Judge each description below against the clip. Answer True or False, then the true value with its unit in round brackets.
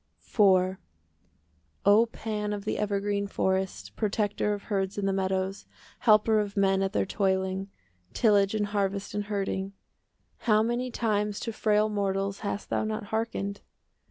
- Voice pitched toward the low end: False (205 Hz)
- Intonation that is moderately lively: False (1.6 semitones)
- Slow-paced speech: False (150 wpm)